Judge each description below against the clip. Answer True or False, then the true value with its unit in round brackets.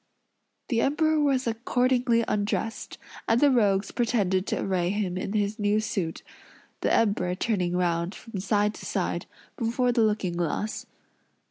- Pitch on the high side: True (210 Hz)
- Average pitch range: True (3.9 semitones)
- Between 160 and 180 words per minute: False (145 wpm)